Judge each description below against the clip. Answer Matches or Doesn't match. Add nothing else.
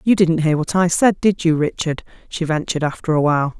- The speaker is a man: Doesn't match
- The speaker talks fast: Matches